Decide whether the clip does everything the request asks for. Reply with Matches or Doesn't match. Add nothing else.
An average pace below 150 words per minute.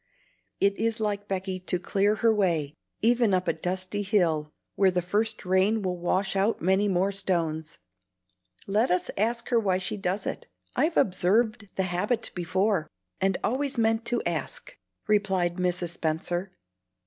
Doesn't match